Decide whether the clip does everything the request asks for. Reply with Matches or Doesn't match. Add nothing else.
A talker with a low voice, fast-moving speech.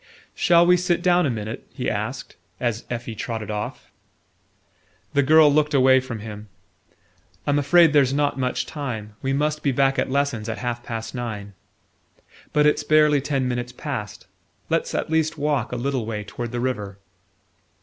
Doesn't match